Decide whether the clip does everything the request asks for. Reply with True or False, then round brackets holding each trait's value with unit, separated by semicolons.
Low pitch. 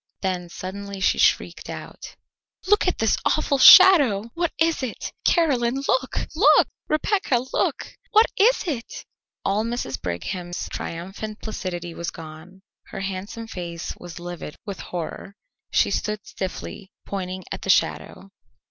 False (200 Hz)